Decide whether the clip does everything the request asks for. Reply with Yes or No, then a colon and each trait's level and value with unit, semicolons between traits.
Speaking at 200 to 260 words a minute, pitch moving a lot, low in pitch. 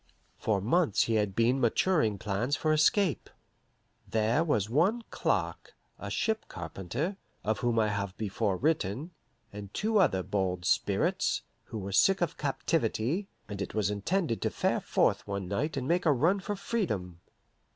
No: average, 160 wpm; wide, 8.6 semitones; low, 115 Hz